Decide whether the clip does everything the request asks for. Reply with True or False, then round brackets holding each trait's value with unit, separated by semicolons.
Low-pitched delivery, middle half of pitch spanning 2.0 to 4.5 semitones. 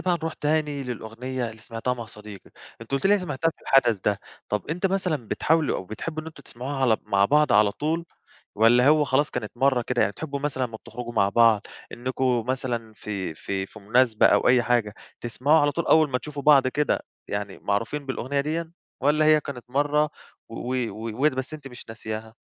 False (130 Hz; 4.9 semitones)